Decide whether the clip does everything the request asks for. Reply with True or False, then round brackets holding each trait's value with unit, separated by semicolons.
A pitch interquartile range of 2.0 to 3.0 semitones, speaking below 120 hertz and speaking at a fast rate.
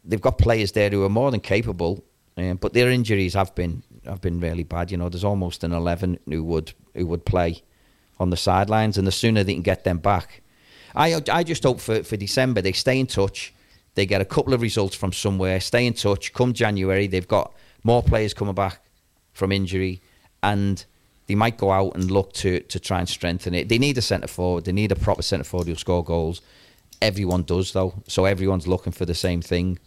True (2.7 semitones; 95 Hz; 220 wpm)